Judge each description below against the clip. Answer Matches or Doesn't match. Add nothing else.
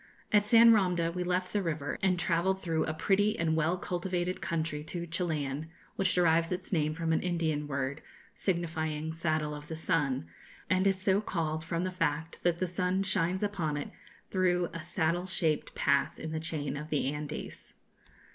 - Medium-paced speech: Matches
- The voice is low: Doesn't match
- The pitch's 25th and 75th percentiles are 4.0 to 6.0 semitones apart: Doesn't match